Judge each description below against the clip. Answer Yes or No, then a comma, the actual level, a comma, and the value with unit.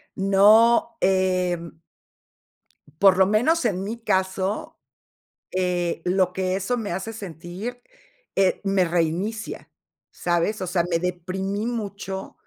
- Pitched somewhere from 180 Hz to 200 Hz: Yes, high, 190 Hz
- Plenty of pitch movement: No, average, 2.8 semitones